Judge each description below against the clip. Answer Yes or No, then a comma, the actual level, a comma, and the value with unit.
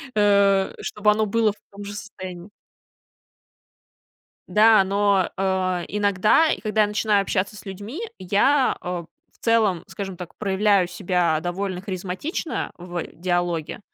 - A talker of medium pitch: No, high, 200 Hz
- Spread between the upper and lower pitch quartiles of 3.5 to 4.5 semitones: No, narrow, 2.5 semitones